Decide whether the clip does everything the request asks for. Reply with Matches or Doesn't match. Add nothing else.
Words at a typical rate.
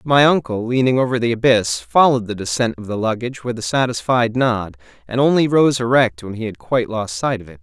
Doesn't match